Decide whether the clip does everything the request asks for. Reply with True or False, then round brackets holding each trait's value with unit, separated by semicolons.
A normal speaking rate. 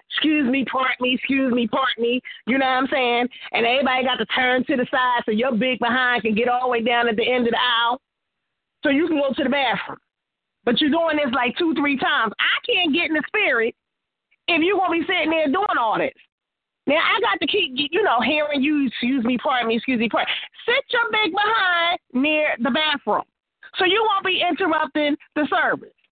False (225 wpm)